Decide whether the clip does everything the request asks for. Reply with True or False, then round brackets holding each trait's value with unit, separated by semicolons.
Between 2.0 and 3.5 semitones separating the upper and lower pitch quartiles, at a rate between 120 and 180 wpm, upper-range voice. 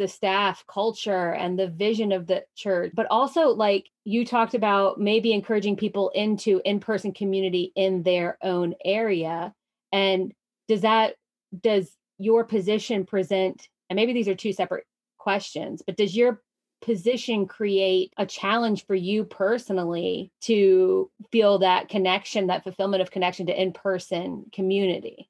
True (2.7 semitones; 145 wpm; 200 Hz)